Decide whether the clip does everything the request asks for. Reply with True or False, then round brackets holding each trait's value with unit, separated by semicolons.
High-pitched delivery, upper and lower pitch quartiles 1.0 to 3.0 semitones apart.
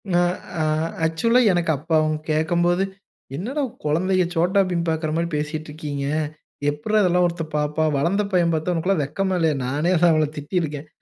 False (165 Hz; 2.7 semitones)